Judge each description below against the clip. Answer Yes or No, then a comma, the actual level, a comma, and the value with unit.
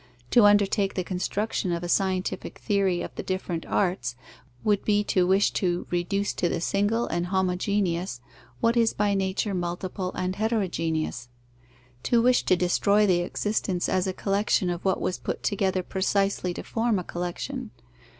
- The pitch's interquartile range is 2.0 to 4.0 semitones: Yes, narrow, 2.5 semitones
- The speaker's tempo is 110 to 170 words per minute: Yes, average, 160 wpm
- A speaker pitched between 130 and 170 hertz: No, high, 190 Hz